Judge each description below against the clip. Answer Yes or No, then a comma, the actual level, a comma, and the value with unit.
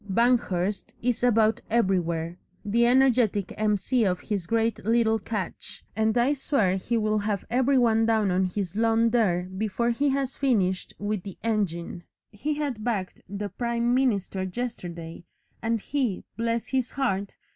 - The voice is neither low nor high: No, high, 220 Hz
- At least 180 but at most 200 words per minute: No, average, 150 wpm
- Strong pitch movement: No, average, 3.8 semitones